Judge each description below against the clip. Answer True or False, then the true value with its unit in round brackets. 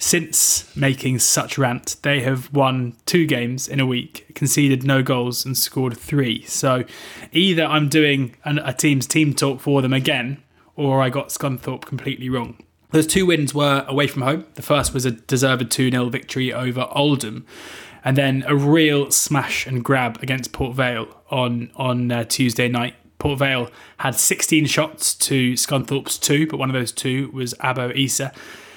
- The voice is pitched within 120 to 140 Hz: True (135 Hz)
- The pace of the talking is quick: False (170 wpm)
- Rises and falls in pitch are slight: True (2.3 semitones)